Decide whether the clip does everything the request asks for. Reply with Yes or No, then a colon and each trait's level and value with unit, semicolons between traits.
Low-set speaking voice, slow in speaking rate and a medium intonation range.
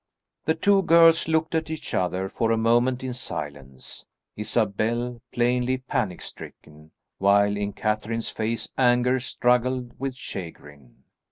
Yes: low, 120 Hz; slow, 125 wpm; average, 4.2 semitones